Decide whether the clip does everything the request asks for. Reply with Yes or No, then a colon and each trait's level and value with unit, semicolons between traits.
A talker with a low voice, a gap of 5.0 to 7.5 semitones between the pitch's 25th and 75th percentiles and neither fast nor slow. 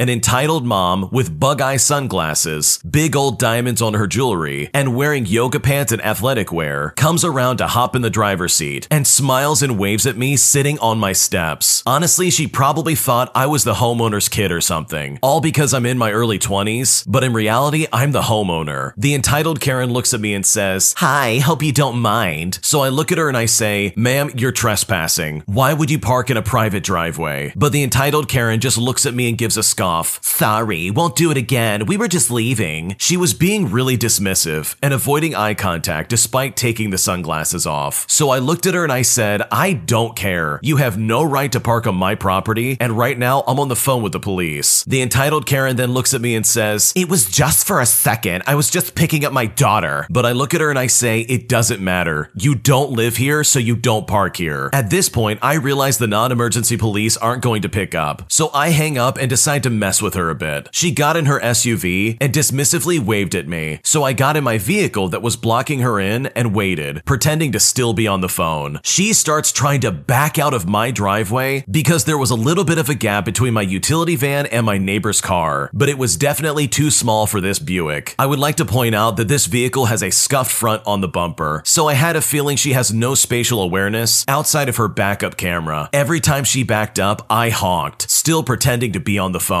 No: low, 120 Hz; average, 5.3 semitones; fast, 225 wpm